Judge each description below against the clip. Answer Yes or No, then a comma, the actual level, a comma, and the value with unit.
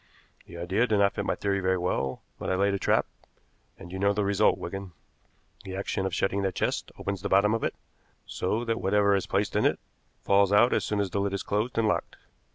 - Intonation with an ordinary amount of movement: No, narrow, 1.3 semitones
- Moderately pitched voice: No, low, 100 Hz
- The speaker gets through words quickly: Yes, fast, 235 wpm